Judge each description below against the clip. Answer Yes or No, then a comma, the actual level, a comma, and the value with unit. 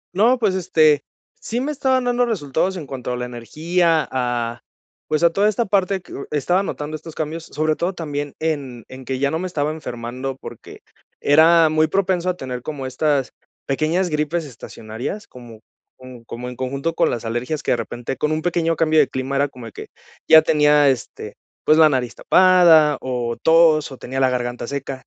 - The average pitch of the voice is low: No, medium, 150 Hz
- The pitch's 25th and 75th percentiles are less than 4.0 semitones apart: No, average, 4.6 semitones